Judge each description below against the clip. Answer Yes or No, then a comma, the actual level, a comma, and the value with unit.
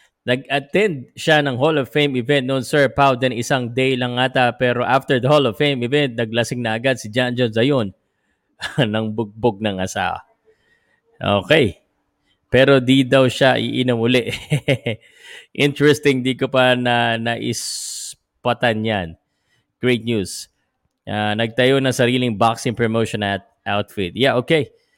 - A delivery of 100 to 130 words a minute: No, average, 140 wpm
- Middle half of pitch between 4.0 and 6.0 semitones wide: No, average, 2.9 semitones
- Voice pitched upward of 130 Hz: No, low, 125 Hz